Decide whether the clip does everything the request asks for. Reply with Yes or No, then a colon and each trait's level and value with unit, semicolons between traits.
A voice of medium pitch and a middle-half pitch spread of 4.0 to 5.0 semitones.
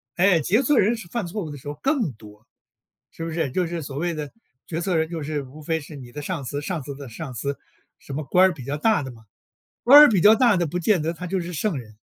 Yes: medium, 160 Hz; average, 4.7 semitones